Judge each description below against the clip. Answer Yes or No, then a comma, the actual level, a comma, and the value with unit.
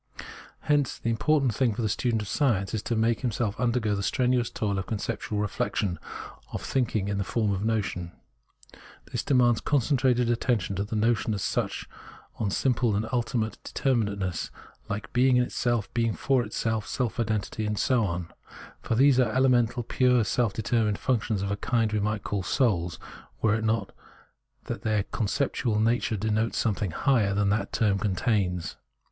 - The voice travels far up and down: No, average, 3.1 semitones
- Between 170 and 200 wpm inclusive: Yes, average, 175 wpm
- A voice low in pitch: Yes, low, 110 Hz